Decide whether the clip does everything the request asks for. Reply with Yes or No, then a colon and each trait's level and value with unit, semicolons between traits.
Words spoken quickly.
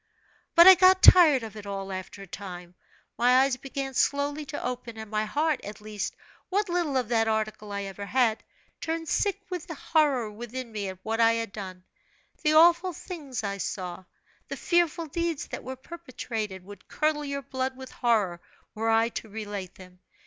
No: average, 185 wpm